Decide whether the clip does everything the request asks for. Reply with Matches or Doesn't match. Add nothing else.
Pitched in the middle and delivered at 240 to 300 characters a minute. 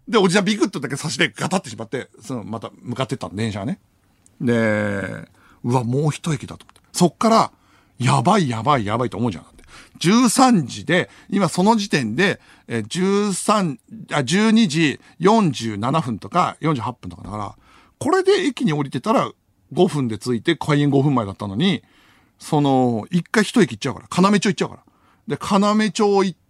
Doesn't match